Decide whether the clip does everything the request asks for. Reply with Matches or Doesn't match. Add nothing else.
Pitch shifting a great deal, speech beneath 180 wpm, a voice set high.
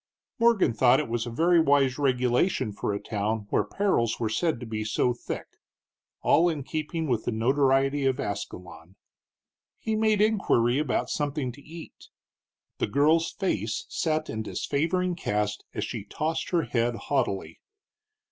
Doesn't match